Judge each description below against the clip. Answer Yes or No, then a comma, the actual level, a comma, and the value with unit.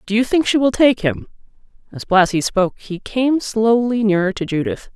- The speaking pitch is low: No, high, 210 Hz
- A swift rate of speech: No, average, 195 wpm